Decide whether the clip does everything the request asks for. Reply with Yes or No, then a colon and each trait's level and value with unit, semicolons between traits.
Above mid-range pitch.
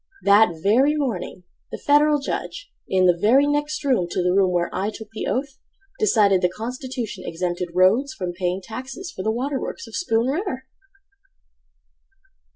Yes: high, 225 Hz